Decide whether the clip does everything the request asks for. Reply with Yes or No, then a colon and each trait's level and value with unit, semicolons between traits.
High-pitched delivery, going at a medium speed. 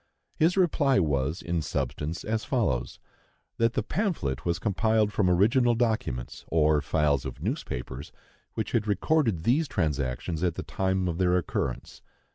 No: very low, 90 Hz; average, 145 wpm